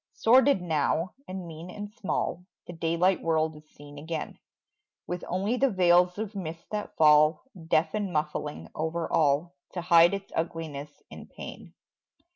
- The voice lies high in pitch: No, medium, 170 Hz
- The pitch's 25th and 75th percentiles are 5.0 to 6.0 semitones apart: No, average, 3.2 semitones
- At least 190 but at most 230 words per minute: No, average, 150 wpm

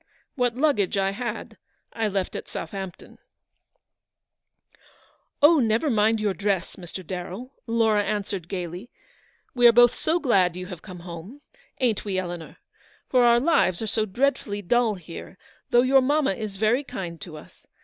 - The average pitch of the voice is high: Yes, high, 210 Hz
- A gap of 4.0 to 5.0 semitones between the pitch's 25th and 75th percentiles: Yes, average, 4.6 semitones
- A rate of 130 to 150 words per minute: No, average, 165 wpm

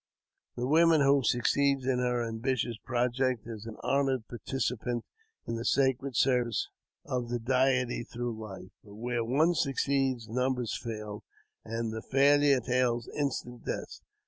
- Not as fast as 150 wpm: Yes, average, 140 wpm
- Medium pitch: No, low, 125 Hz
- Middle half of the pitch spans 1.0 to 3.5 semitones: Yes, narrow, 2.5 semitones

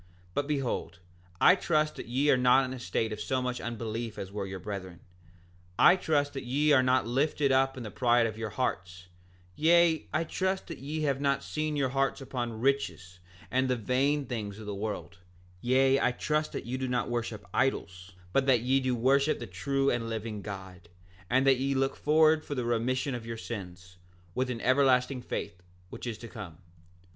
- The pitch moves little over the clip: No, average, 4.0 semitones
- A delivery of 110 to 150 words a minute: No, average, 200 wpm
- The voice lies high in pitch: No, low, 125 Hz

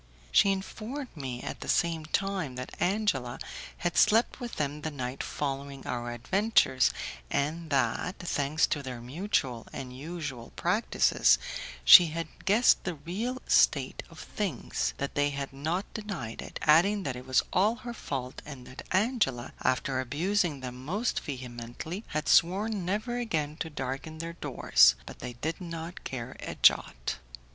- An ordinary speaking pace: Yes, average, 155 wpm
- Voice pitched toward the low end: No, medium, 155 Hz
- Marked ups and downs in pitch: Yes, wide, 6.6 semitones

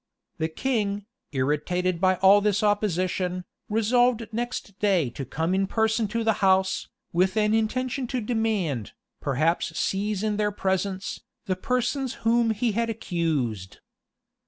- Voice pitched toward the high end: Yes, high, 205 Hz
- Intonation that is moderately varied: Yes, average, 3.7 semitones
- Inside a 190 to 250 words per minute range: No, average, 140 wpm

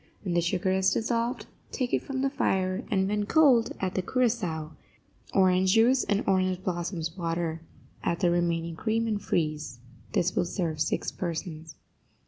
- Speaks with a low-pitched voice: No, medium, 185 Hz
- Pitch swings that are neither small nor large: Yes, average, 4.4 semitones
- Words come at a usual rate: Yes, average, 160 wpm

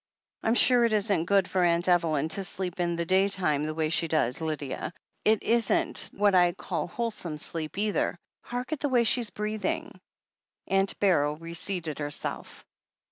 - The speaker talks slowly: No, average, 180 wpm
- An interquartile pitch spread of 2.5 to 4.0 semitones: No, average, 4.5 semitones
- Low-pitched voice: No, medium, 185 Hz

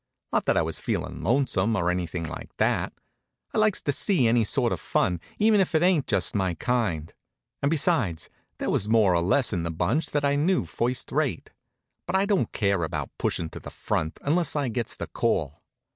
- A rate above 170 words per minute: Yes, fast, 205 wpm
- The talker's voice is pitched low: Yes, low, 115 Hz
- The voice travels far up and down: Yes, wide, 8.8 semitones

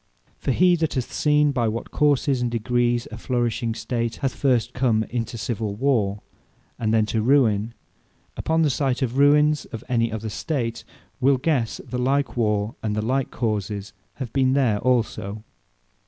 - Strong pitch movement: No, average, 3.5 semitones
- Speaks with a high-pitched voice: No, low, 120 Hz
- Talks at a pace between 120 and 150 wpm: No, average, 170 wpm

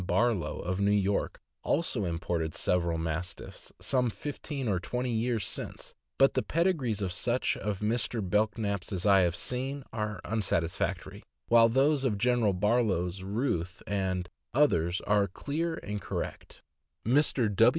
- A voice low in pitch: Yes, low, 105 Hz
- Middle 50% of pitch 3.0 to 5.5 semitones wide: Yes, average, 5.1 semitones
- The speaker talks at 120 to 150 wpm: Yes, average, 140 wpm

